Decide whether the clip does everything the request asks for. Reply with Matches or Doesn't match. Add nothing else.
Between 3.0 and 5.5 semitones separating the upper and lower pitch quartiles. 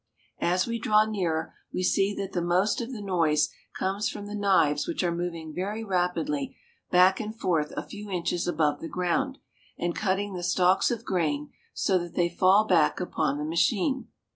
Matches